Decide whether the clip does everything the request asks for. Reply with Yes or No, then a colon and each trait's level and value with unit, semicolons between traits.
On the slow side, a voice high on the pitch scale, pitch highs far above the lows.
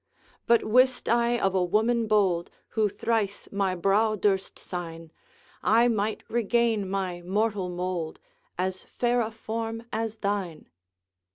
No: slow, 130 wpm; high, 210 Hz; average, 3.4 semitones